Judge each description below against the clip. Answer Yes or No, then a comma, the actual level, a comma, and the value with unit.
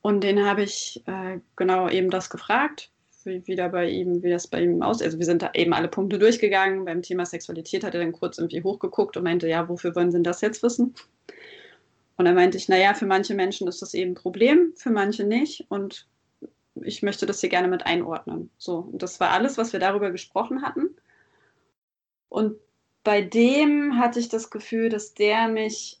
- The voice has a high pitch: Yes, high, 195 Hz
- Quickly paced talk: Yes, fast, 210 wpm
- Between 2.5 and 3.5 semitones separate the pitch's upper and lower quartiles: No, average, 3.9 semitones